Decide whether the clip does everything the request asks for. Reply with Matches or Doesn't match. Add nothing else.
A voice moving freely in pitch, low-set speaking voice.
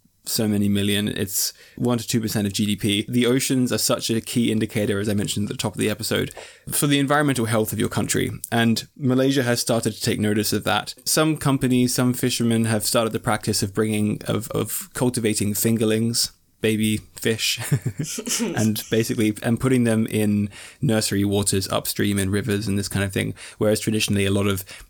Doesn't match